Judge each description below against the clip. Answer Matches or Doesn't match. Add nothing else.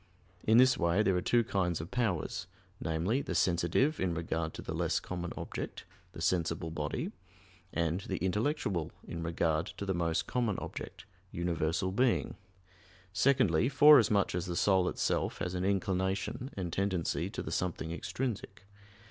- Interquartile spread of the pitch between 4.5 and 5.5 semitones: Doesn't match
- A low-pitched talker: Matches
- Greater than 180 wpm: Doesn't match